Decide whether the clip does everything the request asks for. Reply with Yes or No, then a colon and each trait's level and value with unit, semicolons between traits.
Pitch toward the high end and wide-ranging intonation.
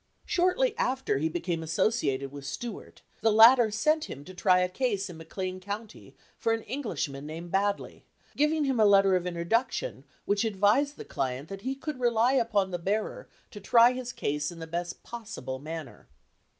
Yes: high, 200 Hz; wide, 5.9 semitones